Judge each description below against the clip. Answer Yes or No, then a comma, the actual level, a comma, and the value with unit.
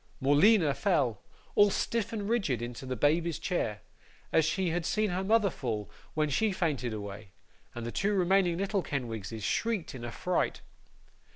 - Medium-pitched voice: Yes, medium, 160 Hz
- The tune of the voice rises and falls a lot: Yes, wide, 8.6 semitones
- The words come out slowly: No, average, 160 wpm